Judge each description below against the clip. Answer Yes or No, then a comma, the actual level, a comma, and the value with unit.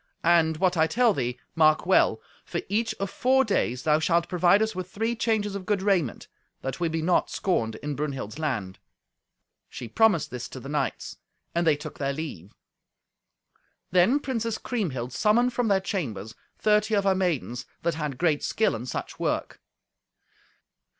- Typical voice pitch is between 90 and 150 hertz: No, medium, 170 Hz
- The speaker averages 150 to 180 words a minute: Yes, average, 170 wpm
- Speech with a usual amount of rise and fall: No, wide, 6.7 semitones